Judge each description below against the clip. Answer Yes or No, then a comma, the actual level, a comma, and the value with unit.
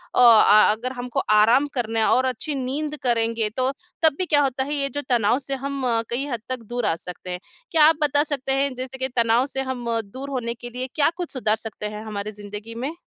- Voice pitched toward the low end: No, very high, 255 Hz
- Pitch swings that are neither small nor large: Yes, average, 3.5 semitones